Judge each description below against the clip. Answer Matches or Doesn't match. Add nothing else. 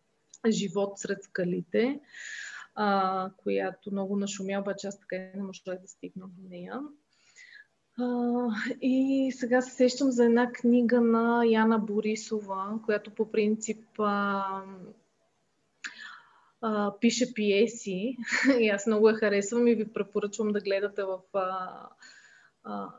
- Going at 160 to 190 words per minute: Doesn't match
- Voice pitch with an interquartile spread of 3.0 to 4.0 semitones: Matches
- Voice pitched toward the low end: Doesn't match